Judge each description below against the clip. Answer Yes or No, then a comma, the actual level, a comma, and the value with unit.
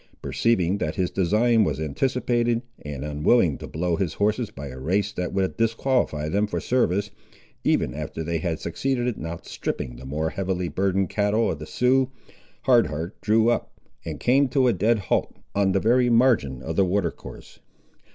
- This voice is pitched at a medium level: No, low, 100 Hz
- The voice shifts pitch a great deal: Yes, wide, 6.3 semitones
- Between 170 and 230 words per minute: Yes, average, 180 wpm